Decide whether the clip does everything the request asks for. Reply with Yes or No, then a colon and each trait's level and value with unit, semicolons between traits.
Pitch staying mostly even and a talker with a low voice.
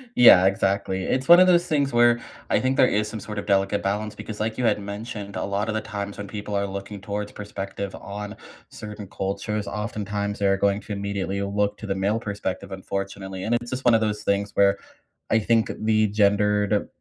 Yes: narrow, 1.6 semitones; low, 105 Hz